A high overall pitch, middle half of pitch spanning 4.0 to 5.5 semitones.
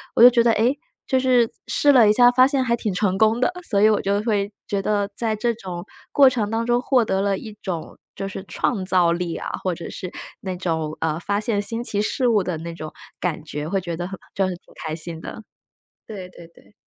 Yes: high, 200 Hz; average, 4.5 semitones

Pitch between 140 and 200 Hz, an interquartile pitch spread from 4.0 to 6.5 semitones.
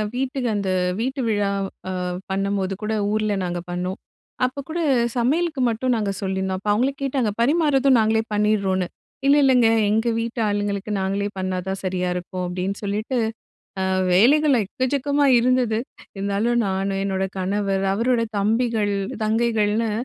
No: high, 215 Hz; average, 4.3 semitones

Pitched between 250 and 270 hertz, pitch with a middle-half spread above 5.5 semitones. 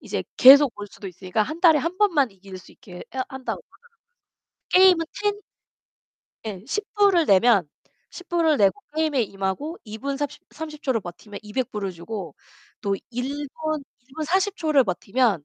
Yes: very high, 260 Hz; wide, 7.9 semitones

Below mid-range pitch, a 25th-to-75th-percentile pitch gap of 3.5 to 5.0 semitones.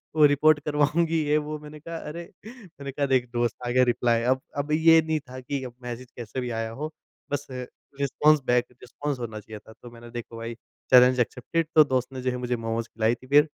Yes: low, 130 Hz; average, 3.9 semitones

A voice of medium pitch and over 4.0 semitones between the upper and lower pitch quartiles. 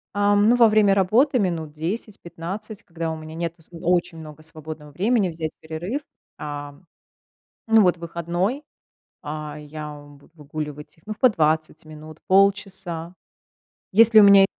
Yes: medium, 170 Hz; average, 4.4 semitones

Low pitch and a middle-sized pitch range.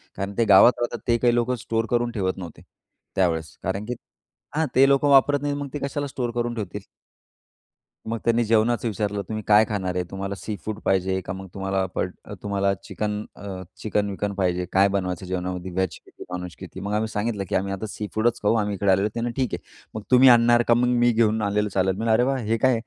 Yes: low, 105 Hz; average, 3.6 semitones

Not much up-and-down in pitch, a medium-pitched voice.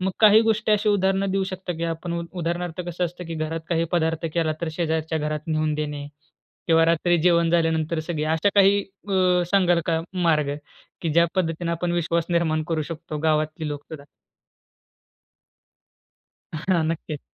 Yes: narrow, 2.2 semitones; medium, 165 Hz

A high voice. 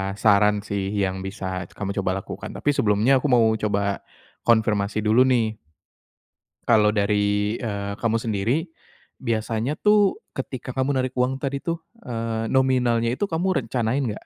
No: low, 115 Hz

